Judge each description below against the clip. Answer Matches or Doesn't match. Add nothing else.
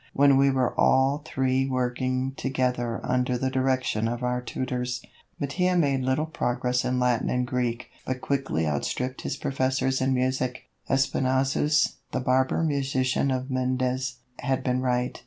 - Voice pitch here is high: Doesn't match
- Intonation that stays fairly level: Matches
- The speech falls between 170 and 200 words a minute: Doesn't match